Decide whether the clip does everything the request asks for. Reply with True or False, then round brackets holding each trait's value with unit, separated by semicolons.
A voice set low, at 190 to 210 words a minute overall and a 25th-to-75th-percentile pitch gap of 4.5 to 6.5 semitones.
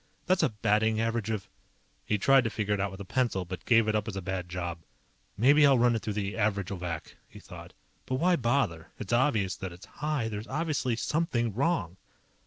True (110 Hz; 205 wpm; 4.8 semitones)